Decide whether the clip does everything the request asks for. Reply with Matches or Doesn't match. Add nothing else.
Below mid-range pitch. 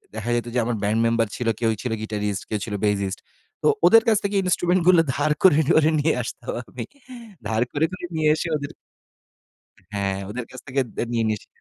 Matches